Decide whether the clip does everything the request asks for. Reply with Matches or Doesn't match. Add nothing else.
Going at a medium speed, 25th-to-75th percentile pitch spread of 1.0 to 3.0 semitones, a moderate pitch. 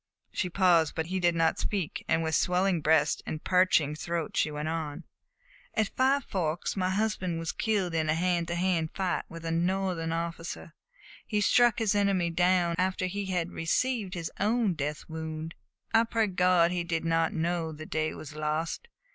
Matches